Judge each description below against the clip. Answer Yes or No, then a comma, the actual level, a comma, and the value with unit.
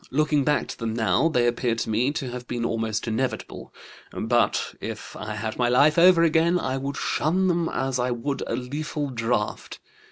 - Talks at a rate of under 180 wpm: No, average, 190 wpm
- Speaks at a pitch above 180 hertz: No, low, 125 Hz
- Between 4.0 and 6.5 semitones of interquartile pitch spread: Yes, average, 4.4 semitones